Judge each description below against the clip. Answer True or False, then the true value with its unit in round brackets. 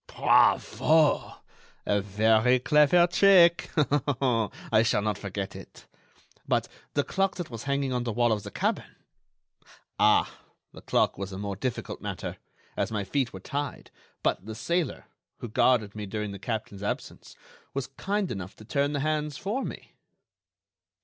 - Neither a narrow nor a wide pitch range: False (6.2 semitones)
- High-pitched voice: False (125 Hz)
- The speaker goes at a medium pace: True (155 wpm)